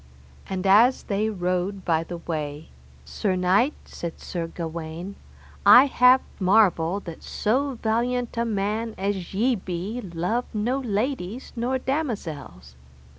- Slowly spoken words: Yes, slow, 125 wpm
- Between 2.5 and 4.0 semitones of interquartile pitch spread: No, wide, 5.4 semitones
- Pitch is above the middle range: Yes, high, 200 Hz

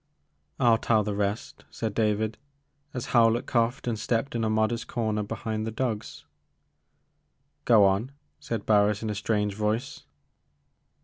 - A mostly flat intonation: Yes, narrow, 1.7 semitones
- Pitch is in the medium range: No, low, 110 Hz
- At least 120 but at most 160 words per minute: Yes, average, 145 wpm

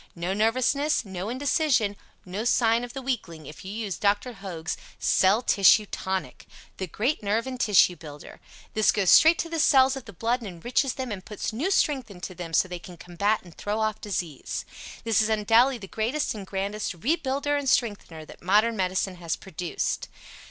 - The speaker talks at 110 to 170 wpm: No, average, 185 wpm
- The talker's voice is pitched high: Yes, high, 210 Hz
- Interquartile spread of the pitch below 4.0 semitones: No, average, 4.9 semitones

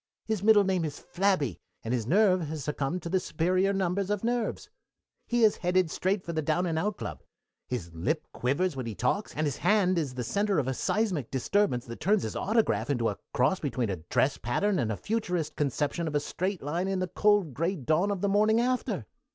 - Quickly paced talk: Yes, fast, 215 wpm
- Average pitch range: No, wide, 6.5 semitones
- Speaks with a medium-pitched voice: Yes, medium, 175 Hz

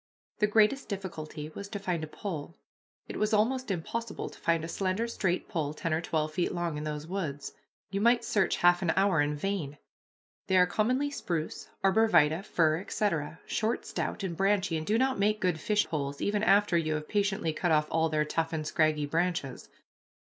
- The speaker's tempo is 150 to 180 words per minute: No, average, 195 wpm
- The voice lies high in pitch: No, medium, 180 Hz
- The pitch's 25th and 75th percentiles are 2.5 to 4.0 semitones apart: No, average, 4.8 semitones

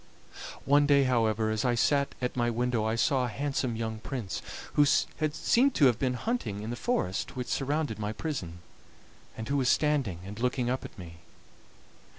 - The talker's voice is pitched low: Yes, low, 125 Hz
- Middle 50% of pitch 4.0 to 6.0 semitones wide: Yes, average, 4.3 semitones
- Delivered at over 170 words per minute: Yes, average, 180 wpm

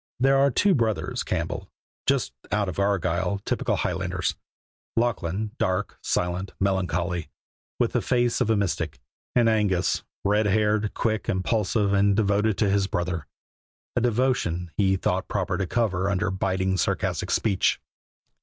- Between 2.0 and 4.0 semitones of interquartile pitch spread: Yes, average, 2.9 semitones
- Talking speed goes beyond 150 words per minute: No, average, 140 wpm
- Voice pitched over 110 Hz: No, low, 100 Hz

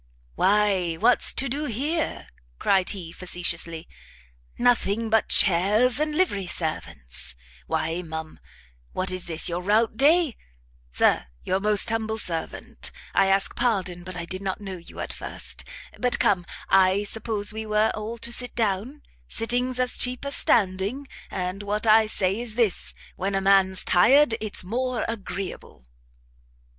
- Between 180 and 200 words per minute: No, average, 145 wpm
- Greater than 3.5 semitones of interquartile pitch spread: Yes, average, 4.4 semitones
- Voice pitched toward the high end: Yes, high, 205 Hz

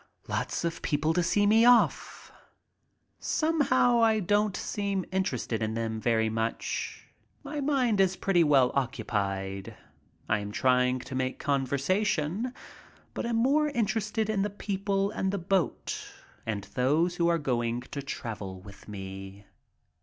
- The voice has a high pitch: No, medium, 165 Hz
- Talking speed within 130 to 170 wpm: Yes, average, 140 wpm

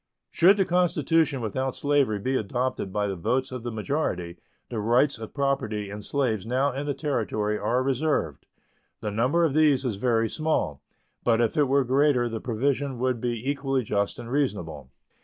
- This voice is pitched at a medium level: No, low, 125 Hz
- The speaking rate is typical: Yes, average, 175 wpm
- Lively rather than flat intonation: No, average, 4.5 semitones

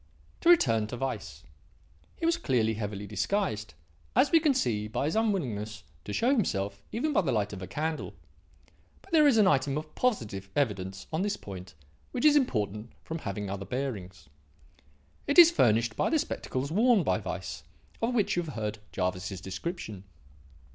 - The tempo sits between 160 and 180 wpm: Yes, average, 170 wpm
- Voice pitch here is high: No, low, 120 Hz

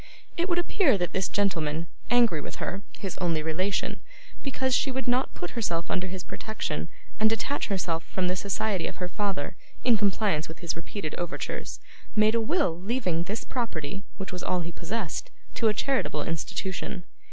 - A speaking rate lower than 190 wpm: Yes, average, 175 wpm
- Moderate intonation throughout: Yes, average, 4.8 semitones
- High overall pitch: Yes, high, 195 Hz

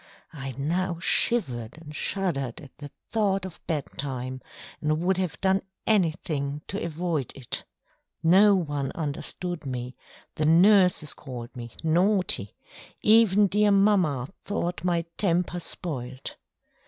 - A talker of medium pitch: Yes, medium, 165 Hz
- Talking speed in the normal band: No, slow, 125 wpm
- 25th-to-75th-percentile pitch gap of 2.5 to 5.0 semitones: No, wide, 5.4 semitones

